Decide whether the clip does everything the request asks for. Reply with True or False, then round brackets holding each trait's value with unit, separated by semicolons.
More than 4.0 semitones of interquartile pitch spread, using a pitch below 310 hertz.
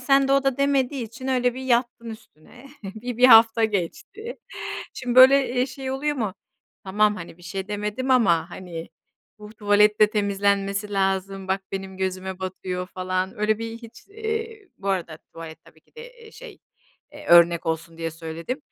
True (5.4 semitones; 210 Hz)